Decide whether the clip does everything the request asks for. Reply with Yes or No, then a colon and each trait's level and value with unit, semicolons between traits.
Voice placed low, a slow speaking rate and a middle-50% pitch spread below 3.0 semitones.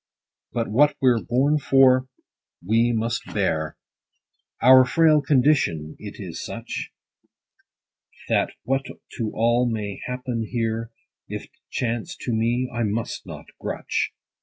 Yes: low, 120 Hz; slow, 120 wpm; narrow, 2.6 semitones